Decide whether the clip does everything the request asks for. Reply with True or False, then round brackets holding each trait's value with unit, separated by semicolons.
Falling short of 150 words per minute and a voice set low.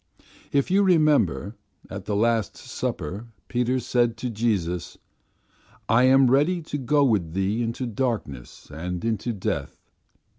True (135 wpm; 115 Hz)